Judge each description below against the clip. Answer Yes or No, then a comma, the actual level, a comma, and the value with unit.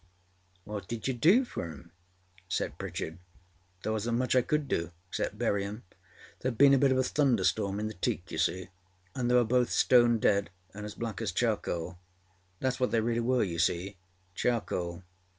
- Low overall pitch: Yes, low, 110 Hz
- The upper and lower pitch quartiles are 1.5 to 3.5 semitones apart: No, average, 5.0 semitones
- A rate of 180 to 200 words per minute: Yes, average, 185 wpm